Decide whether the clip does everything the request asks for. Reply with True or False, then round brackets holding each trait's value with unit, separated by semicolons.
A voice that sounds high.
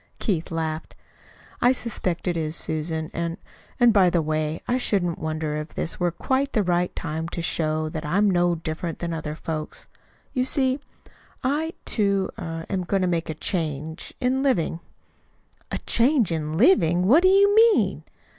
False (175 Hz)